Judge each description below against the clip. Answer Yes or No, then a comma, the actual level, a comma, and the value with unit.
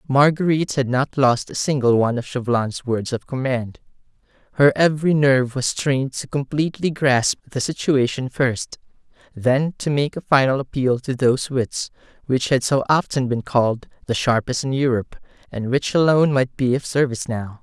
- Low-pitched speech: Yes, low, 130 Hz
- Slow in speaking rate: No, average, 170 wpm